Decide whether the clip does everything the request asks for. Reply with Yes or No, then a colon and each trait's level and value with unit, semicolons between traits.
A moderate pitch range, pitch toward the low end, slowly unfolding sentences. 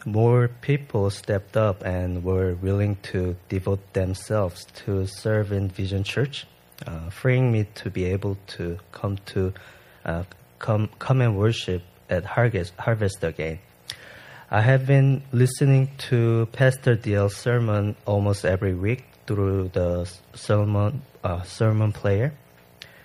Yes: average, 4.0 semitones; low, 100 Hz; slow, 130 wpm